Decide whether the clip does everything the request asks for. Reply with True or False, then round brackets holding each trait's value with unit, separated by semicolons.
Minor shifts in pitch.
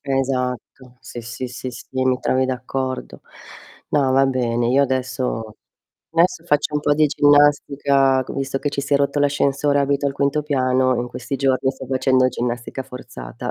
True (1.7 semitones)